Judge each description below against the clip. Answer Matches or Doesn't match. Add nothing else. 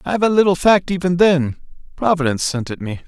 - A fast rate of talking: Matches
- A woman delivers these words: Doesn't match